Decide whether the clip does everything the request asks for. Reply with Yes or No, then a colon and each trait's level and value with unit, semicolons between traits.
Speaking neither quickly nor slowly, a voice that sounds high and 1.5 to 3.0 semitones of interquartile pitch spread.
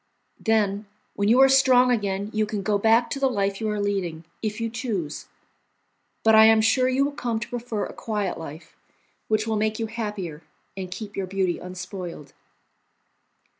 Yes: average, 180 wpm; high, 215 Hz; average, 2.7 semitones